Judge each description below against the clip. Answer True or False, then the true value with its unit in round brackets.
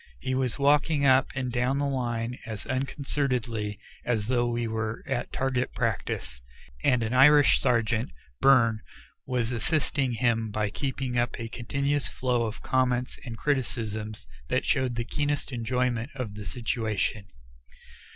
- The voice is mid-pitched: False (125 Hz)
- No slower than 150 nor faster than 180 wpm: False (140 wpm)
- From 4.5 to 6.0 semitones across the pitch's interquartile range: False (2.7 semitones)